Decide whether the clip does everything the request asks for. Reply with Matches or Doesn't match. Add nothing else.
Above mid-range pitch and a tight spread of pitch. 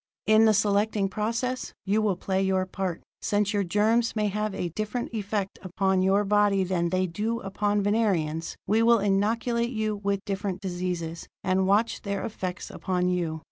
Matches